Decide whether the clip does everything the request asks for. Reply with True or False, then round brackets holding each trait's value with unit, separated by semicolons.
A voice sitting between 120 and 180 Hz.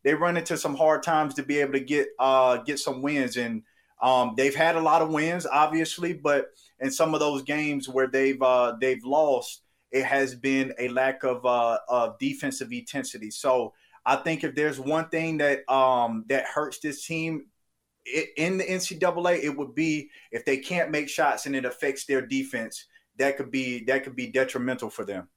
True (140 Hz)